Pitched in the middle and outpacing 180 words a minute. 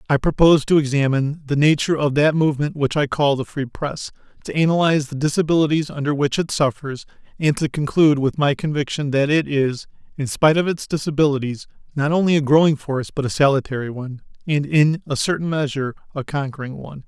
Yes: medium, 145 Hz; average, 190 wpm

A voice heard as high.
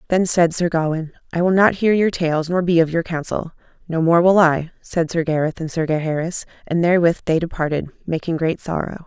No: medium, 165 Hz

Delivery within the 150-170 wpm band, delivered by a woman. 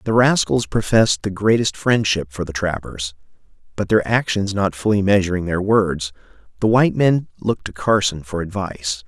No: average, 165 wpm; male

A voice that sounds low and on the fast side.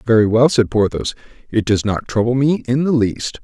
Yes: low, 115 Hz; fast, 210 wpm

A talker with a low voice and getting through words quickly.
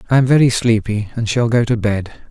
Yes: low, 115 Hz; fast, 235 wpm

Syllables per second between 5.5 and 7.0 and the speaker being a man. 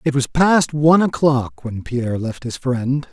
No: 4.3 syllables/s; male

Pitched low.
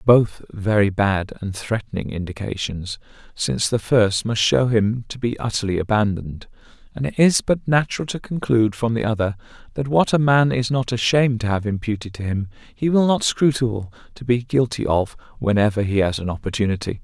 Yes: low, 115 Hz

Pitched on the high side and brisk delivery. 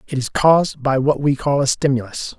No: medium, 140 Hz; fast, 225 wpm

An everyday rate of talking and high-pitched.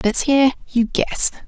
Yes: average, 160 wpm; very high, 250 Hz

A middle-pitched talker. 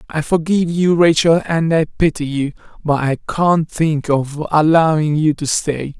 Yes: medium, 155 Hz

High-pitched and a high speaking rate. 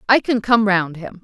Yes: high, 205 Hz; fast, 245 wpm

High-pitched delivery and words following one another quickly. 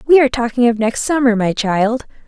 Yes: high, 240 Hz; fast, 210 wpm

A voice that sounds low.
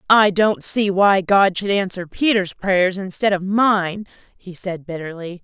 No: high, 190 Hz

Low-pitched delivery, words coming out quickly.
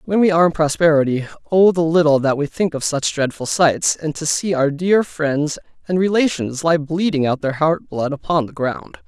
No: medium, 160 Hz; fast, 210 wpm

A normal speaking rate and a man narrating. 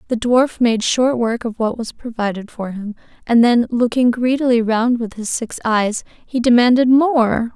No: average, 185 wpm; female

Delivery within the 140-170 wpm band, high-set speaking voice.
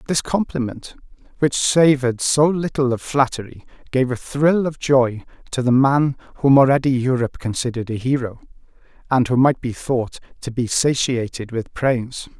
No: average, 155 wpm; low, 130 Hz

